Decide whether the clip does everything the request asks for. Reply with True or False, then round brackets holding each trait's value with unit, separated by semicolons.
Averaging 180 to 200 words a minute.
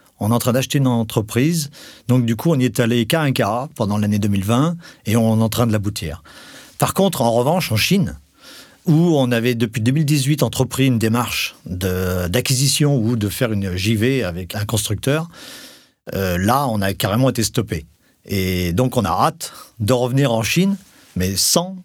True (190 wpm)